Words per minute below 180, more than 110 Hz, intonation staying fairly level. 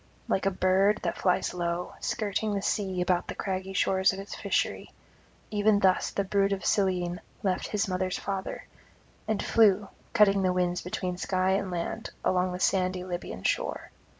Yes: average, 170 wpm; high, 190 Hz; narrow, 1.6 semitones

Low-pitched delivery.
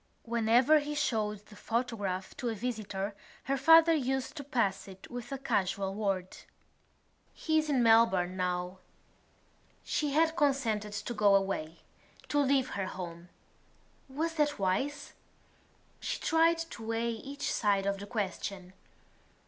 No: high, 225 Hz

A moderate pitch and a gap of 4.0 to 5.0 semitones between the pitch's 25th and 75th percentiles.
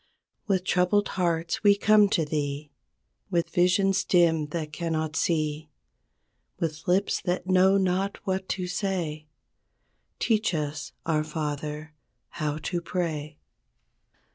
No: medium, 170 Hz; average, 3.6 semitones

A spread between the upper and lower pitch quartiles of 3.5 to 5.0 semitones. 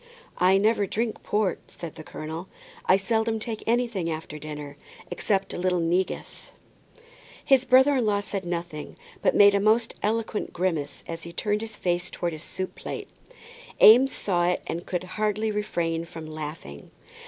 Yes: average, 4.4 semitones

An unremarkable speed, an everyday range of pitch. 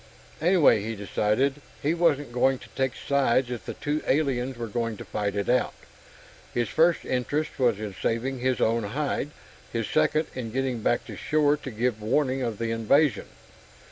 Yes: average, 175 wpm; average, 3.9 semitones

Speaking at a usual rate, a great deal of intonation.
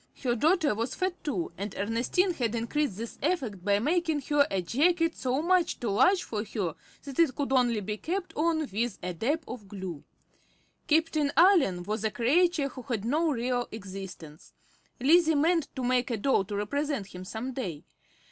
Yes: average, 180 wpm; wide, 7.1 semitones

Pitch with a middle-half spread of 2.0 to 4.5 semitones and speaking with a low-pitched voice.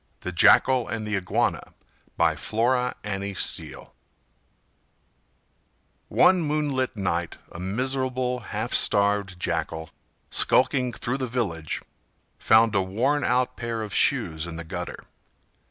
No: wide, 5.4 semitones; low, 110 Hz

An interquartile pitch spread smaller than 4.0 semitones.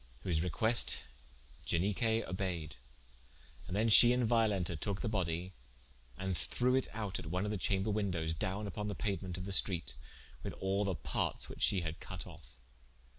Yes: average, 3.2 semitones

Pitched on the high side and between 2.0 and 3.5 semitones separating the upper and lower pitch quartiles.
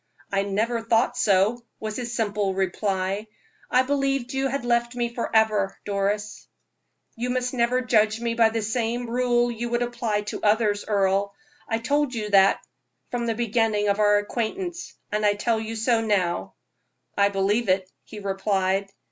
Yes: high, 220 Hz; average, 2.8 semitones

